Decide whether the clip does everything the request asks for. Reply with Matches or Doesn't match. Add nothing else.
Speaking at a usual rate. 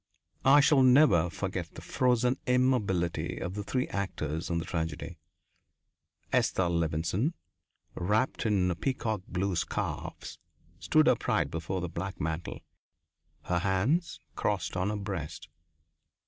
Doesn't match